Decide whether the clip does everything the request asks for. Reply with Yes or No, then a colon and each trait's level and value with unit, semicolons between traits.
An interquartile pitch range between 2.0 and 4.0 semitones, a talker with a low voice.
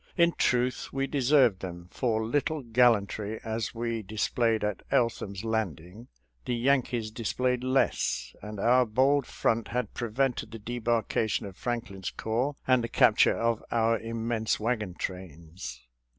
Yes: average, 2.8 semitones; low, 115 Hz